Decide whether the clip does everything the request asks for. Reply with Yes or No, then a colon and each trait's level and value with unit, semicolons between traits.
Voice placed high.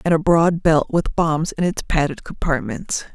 No: medium, 160 Hz